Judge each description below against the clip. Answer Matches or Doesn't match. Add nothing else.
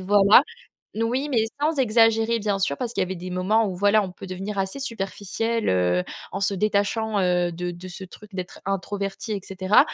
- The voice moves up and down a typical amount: Matches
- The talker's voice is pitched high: Matches